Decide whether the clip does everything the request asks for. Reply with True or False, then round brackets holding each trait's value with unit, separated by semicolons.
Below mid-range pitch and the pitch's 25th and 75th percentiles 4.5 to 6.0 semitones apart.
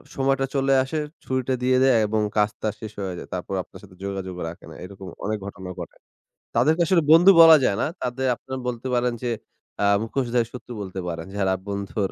True (120 Hz; 5.1 semitones)